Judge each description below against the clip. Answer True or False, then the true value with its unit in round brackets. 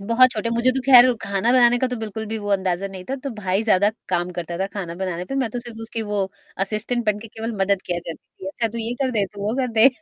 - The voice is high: True (215 Hz)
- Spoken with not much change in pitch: False (3.6 semitones)